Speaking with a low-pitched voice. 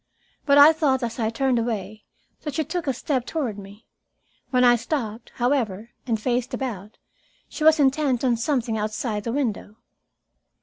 No: high, 245 Hz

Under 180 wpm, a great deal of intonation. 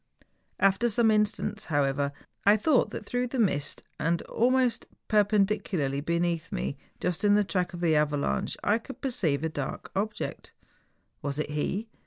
Yes: average, 155 wpm; wide, 6.2 semitones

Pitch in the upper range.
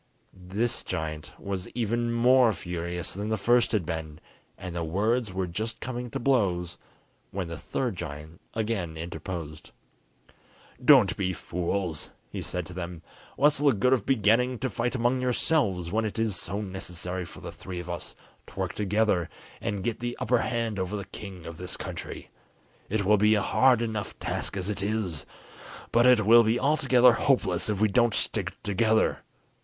No: low, 105 Hz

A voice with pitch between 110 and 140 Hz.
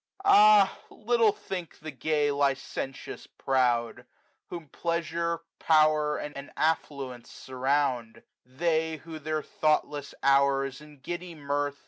No: medium, 150 Hz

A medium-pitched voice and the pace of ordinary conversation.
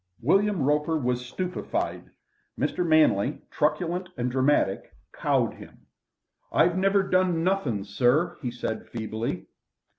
No: medium, 150 Hz; slow, 115 wpm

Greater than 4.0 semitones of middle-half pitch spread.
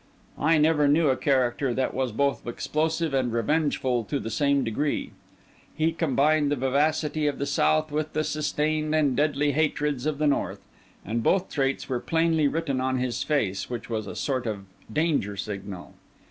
No: average, 3.5 semitones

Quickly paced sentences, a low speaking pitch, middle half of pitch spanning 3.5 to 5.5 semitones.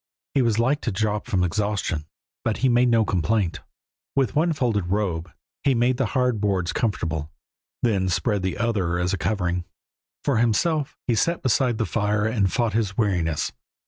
No: average, 175 wpm; low, 105 Hz; average, 4.3 semitones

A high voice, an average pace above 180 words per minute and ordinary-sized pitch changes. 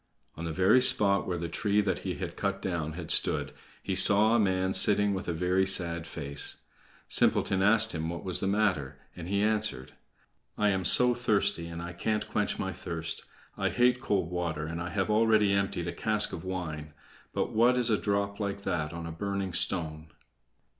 No: very low, 95 Hz; average, 195 wpm; average, 3.5 semitones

